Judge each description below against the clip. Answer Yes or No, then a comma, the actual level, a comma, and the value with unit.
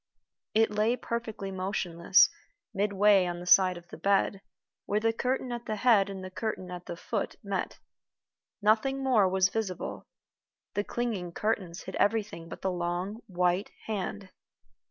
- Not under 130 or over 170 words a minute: Yes, average, 155 wpm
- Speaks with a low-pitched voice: No, high, 200 Hz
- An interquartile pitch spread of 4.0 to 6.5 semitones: No, average, 3.2 semitones